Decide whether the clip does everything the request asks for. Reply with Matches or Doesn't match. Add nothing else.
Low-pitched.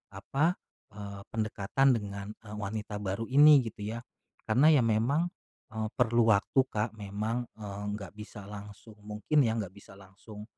Matches